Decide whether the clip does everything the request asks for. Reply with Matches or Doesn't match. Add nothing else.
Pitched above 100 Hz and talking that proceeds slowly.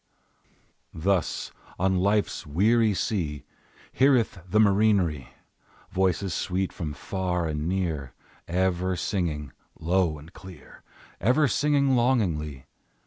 Doesn't match